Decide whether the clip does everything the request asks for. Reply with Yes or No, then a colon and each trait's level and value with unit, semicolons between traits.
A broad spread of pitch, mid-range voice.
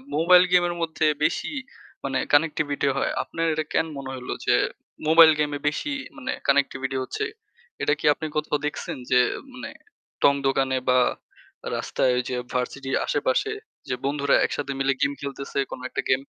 No: average, 2.9 semitones; medium, 145 Hz